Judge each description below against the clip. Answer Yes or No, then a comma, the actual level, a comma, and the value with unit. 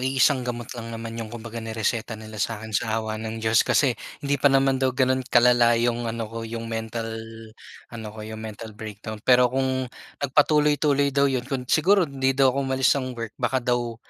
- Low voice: Yes, low, 120 Hz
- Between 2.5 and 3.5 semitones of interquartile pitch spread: Yes, average, 2.8 semitones